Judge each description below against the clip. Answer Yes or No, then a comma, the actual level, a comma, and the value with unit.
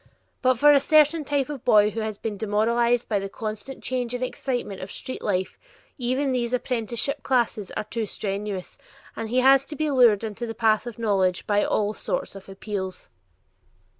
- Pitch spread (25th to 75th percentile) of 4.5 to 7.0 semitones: No, average, 3.6 semitones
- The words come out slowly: No, average, 185 wpm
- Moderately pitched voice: No, high, 230 Hz